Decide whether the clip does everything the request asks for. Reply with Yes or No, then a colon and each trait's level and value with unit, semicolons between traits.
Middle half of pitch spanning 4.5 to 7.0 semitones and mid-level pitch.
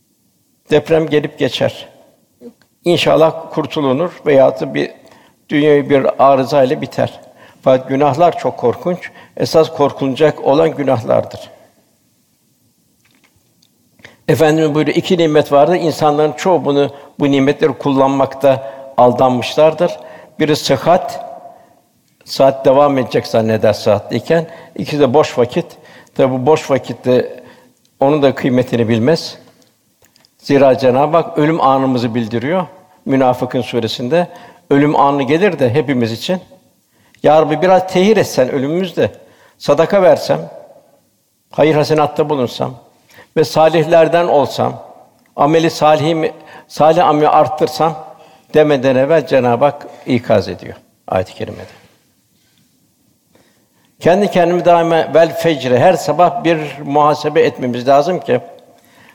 No: average, 3.4 semitones; medium, 150 Hz